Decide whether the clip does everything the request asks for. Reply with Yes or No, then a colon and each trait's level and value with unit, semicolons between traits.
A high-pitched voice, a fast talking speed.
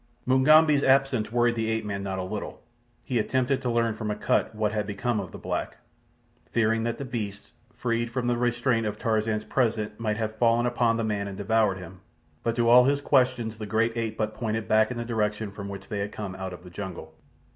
No: low, 110 Hz; fast, 220 wpm